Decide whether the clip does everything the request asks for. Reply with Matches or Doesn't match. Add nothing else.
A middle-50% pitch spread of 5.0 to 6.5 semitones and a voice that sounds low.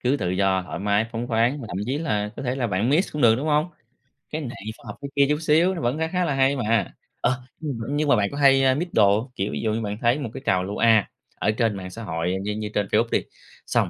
Matches